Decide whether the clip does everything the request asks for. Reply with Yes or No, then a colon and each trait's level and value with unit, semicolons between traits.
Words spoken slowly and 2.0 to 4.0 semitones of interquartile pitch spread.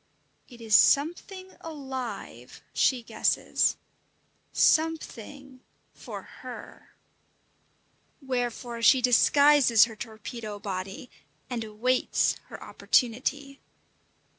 Yes: slow, 80 wpm; average, 3.7 semitones